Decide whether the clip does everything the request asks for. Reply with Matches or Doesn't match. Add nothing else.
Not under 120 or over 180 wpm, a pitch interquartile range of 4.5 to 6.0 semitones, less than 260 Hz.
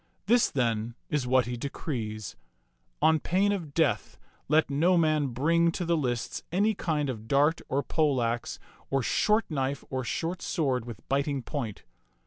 Matches